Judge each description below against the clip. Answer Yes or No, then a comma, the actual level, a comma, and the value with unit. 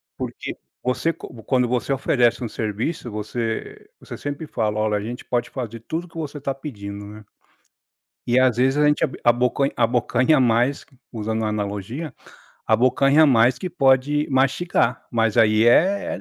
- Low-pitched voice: Yes, low, 125 Hz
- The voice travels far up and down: No, average, 3.8 semitones